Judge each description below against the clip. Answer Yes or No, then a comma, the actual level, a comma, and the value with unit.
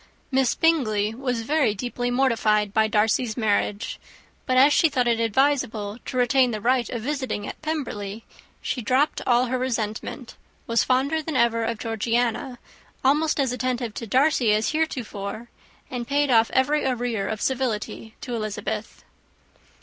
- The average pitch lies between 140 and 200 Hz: No, high, 245 Hz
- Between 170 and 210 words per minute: No, average, 150 wpm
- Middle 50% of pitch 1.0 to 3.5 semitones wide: Yes, average, 3.2 semitones